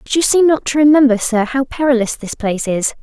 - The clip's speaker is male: No, female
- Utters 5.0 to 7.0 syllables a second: Yes, 5.9 syllables/s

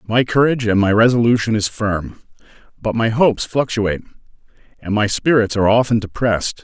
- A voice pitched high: No, low, 110 Hz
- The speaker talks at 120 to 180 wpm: Yes, average, 155 wpm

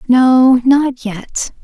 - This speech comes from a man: No, female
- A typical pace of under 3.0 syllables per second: Yes, 2.2 syllables/s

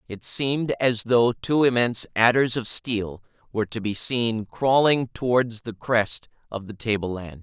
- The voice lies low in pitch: Yes, low, 115 Hz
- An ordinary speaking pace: Yes, average, 170 wpm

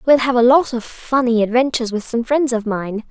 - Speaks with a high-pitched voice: Yes, high, 240 Hz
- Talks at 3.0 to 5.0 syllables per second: No, 5.4 syllables/s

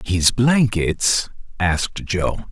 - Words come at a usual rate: No, slow, 95 wpm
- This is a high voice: No, low, 100 Hz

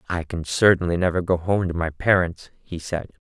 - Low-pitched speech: Yes, very low, 85 Hz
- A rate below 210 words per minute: Yes, average, 200 wpm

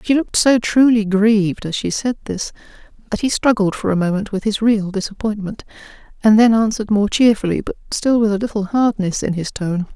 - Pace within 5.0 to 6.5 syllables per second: Yes, 5.6 syllables/s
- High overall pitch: Yes, high, 210 Hz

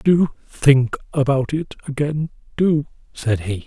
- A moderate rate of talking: No, slow, 115 wpm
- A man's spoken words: Yes, male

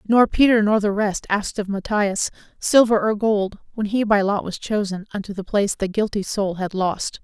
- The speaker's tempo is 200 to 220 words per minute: Yes, fast, 205 wpm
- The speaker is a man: No, female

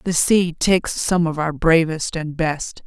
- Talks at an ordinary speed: Yes, average, 190 wpm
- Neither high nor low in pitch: Yes, medium, 165 Hz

